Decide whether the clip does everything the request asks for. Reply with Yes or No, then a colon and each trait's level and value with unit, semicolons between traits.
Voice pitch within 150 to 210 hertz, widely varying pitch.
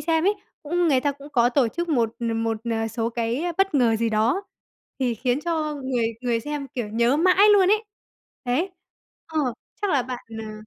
No: very high, 255 Hz; wide, 5.7 semitones